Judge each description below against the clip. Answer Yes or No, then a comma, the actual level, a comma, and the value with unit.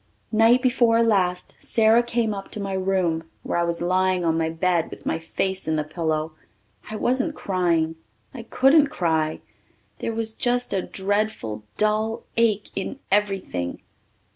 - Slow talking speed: No, average, 155 wpm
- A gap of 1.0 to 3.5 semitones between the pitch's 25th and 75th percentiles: No, average, 5.2 semitones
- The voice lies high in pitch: Yes, high, 195 Hz